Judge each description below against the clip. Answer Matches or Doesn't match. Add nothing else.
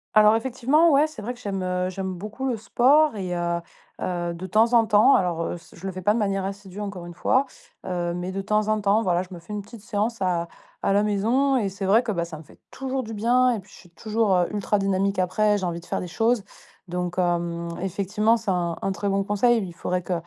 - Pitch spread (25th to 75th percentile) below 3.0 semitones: Doesn't match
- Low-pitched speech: Doesn't match